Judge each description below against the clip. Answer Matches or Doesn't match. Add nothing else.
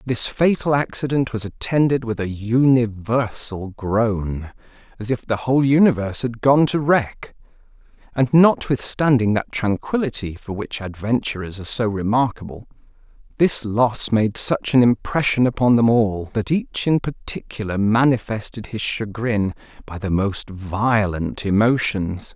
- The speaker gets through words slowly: Matches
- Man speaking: Matches